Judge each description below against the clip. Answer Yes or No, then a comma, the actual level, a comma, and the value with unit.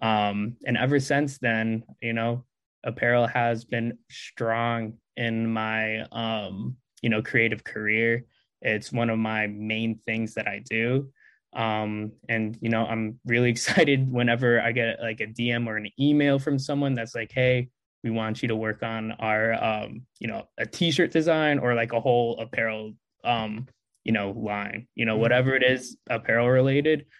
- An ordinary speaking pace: Yes, average, 170 wpm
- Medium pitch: No, low, 115 Hz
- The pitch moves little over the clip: Yes, narrow, 2.0 semitones